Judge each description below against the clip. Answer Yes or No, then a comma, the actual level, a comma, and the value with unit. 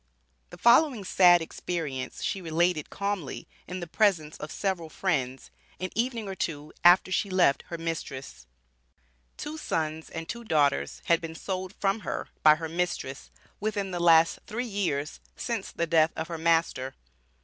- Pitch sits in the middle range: Yes, medium, 170 Hz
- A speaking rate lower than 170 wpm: Yes, average, 160 wpm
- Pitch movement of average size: Yes, average, 3.7 semitones